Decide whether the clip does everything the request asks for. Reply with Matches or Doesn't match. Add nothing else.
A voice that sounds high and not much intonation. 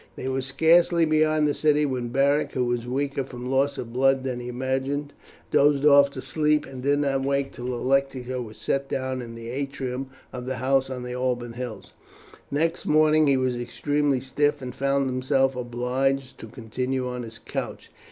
Doesn't match